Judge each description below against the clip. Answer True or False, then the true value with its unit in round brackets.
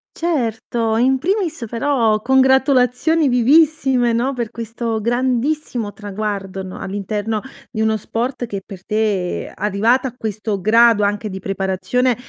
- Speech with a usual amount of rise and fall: True (3.8 semitones)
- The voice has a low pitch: False (230 Hz)